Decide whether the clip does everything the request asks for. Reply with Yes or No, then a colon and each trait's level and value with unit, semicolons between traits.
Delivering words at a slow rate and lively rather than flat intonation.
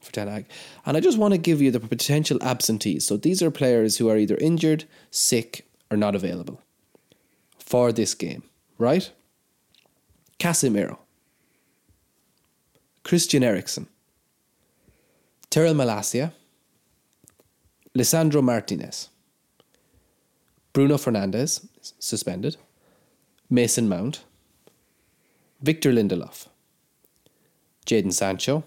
Yes: slow, 90 wpm; wide, 6.1 semitones